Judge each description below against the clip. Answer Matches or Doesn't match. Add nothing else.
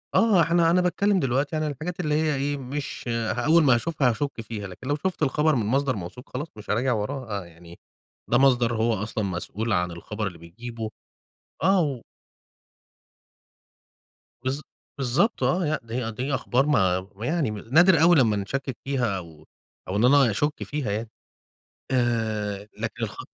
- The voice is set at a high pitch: Doesn't match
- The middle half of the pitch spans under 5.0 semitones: Doesn't match